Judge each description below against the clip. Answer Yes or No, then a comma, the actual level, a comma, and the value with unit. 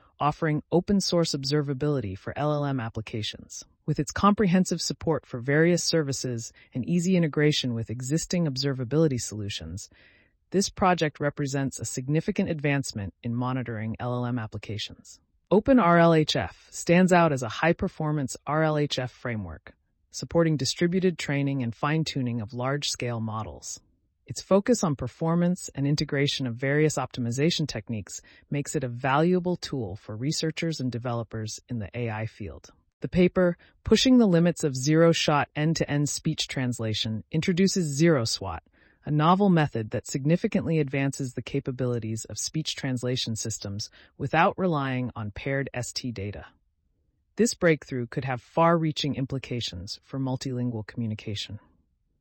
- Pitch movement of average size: No, wide, 5.9 semitones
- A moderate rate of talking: No, slow, 130 wpm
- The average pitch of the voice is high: No, medium, 140 Hz